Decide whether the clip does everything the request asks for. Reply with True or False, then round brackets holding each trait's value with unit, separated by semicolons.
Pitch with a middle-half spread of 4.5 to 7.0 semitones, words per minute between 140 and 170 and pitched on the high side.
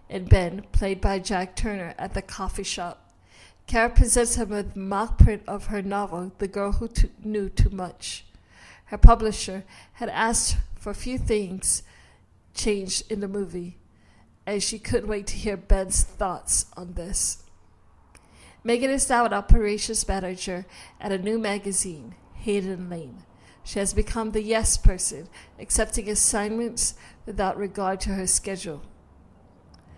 False (4.0 semitones; 150 wpm; 195 Hz)